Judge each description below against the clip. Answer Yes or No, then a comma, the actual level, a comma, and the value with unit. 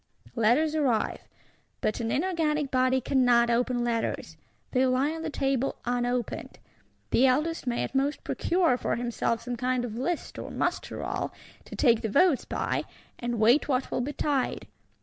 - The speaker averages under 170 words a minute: Yes, average, 160 wpm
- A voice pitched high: Yes, very high, 255 Hz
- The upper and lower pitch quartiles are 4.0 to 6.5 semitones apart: No, average, 3.3 semitones